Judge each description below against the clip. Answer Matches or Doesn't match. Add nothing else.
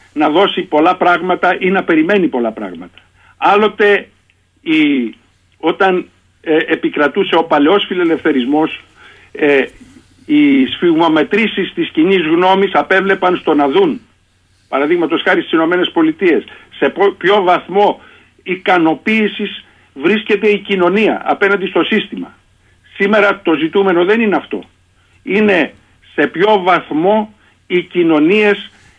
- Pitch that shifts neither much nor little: Matches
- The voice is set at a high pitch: Matches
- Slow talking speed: Matches